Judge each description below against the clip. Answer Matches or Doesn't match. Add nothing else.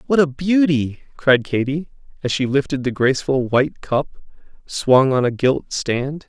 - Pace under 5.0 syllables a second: Matches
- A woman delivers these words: Doesn't match